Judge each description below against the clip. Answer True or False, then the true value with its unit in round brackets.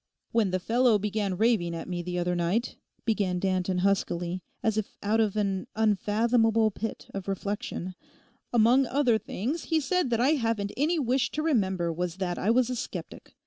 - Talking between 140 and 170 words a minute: False (180 wpm)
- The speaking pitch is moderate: False (215 Hz)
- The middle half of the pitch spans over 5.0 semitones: False (4.3 semitones)